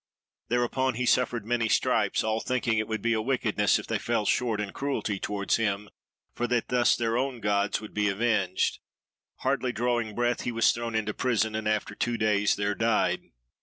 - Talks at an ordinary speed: Yes, average, 190 wpm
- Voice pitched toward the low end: Yes, low, 115 Hz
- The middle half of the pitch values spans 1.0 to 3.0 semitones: Yes, narrow, 2.5 semitones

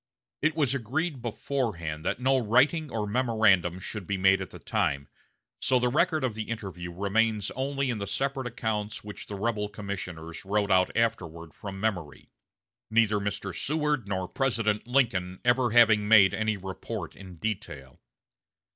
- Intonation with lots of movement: No, average, 4.3 semitones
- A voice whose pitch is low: Yes, low, 105 Hz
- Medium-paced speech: Yes, average, 155 wpm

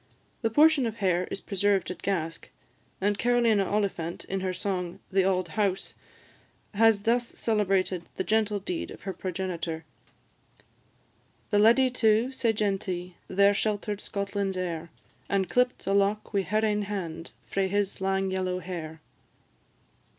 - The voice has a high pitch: Yes, high, 195 Hz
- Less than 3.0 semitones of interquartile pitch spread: Yes, narrow, 2.5 semitones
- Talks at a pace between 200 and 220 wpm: No, average, 145 wpm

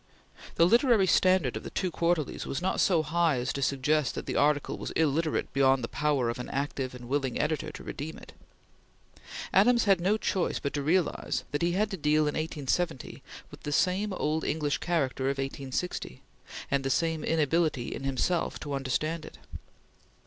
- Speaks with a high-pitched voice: No, medium, 150 Hz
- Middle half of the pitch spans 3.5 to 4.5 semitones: Yes, average, 4.1 semitones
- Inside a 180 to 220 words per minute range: Yes, average, 185 wpm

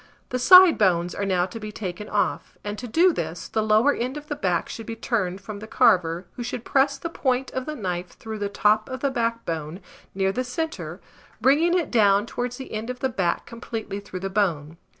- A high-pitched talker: Yes, high, 220 Hz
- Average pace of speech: No, fast, 220 wpm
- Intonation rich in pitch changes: No, average, 4.9 semitones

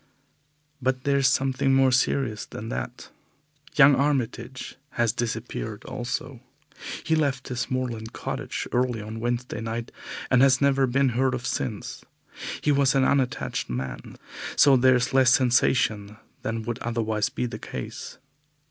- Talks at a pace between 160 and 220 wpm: No, average, 145 wpm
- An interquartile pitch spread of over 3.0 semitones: No, narrow, 2.6 semitones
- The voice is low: Yes, low, 125 Hz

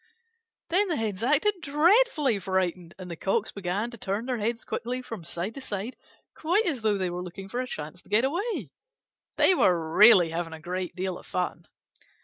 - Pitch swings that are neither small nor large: No, wide, 6.6 semitones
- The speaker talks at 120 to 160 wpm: No, average, 195 wpm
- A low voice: No, high, 210 Hz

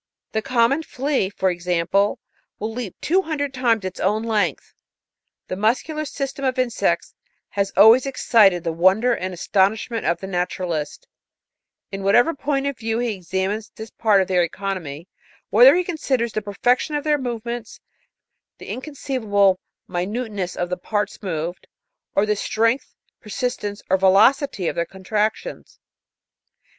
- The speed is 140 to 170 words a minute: Yes, average, 145 wpm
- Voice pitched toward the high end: Yes, high, 215 Hz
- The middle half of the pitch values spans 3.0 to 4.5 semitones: No, average, 5.0 semitones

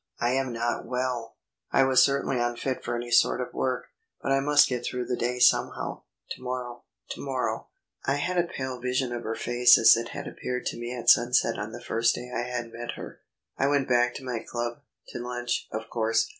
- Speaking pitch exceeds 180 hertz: No, low, 125 Hz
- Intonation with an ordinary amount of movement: No, narrow, 1.3 semitones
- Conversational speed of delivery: No, fast, 215 wpm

